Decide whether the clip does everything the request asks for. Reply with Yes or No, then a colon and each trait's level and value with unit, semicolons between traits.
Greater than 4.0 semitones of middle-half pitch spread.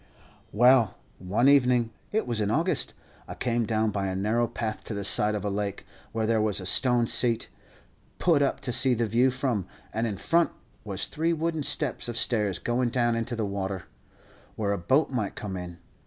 No: average, 3.5 semitones